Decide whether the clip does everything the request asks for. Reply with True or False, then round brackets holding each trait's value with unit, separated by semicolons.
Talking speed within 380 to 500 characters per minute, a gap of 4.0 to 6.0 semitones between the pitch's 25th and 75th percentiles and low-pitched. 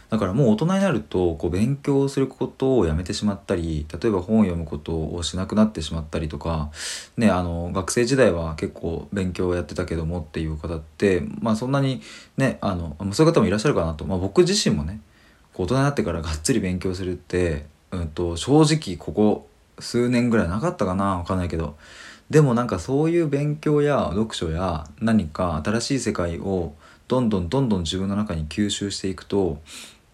True (390 characters per minute; 5.5 semitones; 95 Hz)